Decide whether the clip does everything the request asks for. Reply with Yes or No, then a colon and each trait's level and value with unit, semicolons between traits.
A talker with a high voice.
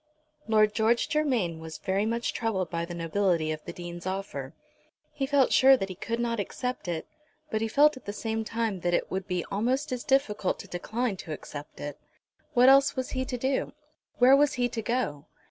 Yes: high, 220 Hz